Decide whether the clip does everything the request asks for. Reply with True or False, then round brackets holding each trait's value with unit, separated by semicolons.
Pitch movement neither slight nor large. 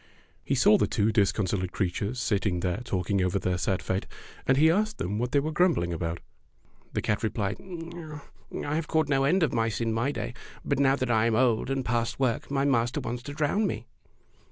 False (6.0 semitones)